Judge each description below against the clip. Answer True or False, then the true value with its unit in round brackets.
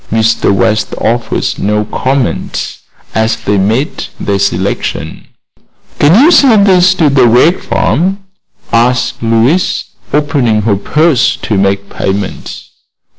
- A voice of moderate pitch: False (115 Hz)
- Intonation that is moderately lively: False (6.6 semitones)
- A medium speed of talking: False (120 wpm)